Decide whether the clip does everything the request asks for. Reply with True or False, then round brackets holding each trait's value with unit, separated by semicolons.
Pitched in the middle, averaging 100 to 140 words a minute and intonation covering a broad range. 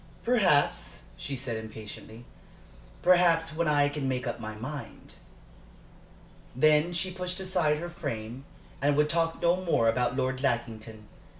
True (145 Hz; 135 wpm; 6.0 semitones)